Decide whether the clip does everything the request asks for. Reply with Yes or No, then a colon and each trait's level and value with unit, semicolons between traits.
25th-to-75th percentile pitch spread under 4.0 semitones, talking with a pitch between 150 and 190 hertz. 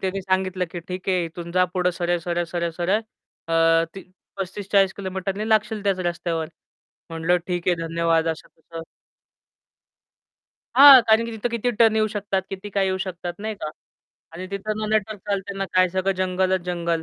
Yes: narrow, 2.6 semitones; medium, 185 Hz